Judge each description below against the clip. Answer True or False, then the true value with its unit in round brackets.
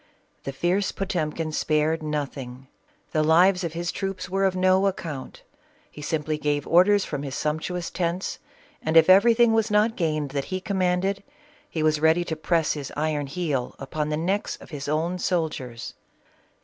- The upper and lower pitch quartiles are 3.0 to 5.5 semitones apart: True (3.6 semitones)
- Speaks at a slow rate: False (170 wpm)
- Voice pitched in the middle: True (165 Hz)